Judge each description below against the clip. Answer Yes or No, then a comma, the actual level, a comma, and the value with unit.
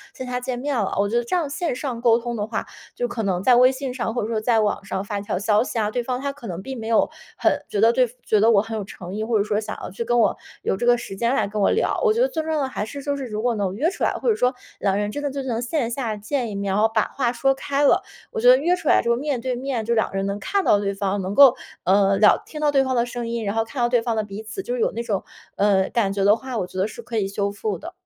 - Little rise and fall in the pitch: No, average, 4.2 semitones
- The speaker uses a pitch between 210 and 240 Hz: Yes, high, 235 Hz